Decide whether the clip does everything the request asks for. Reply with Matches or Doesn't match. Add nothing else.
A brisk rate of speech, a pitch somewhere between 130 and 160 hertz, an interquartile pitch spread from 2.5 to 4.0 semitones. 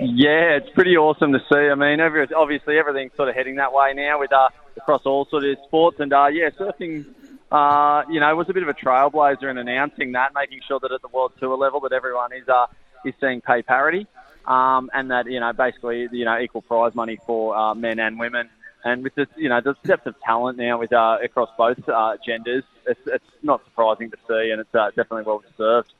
Matches